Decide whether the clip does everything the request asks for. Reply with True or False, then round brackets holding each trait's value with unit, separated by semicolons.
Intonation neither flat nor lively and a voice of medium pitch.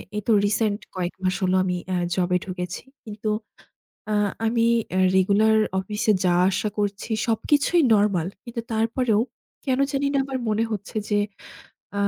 False (3.4 semitones; 210 Hz)